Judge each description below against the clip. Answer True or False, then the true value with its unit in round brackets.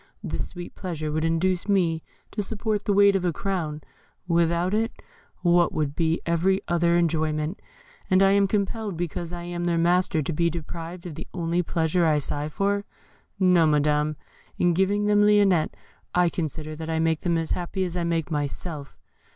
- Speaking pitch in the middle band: True (170 Hz)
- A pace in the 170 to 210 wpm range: True (180 wpm)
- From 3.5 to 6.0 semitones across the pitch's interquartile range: False (2.7 semitones)